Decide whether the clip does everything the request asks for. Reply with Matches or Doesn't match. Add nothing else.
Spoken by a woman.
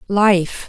Matches